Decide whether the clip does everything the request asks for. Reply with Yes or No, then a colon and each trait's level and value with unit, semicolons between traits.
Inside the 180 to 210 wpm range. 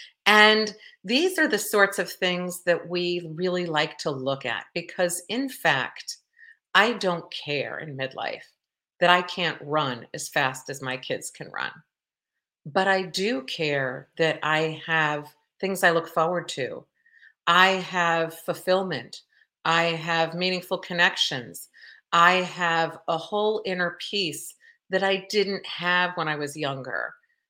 No: average, 145 wpm